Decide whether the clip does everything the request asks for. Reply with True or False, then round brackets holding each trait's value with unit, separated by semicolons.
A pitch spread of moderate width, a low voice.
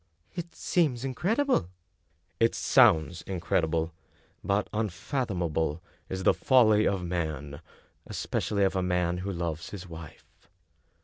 True (4.7 semitones; 90 Hz)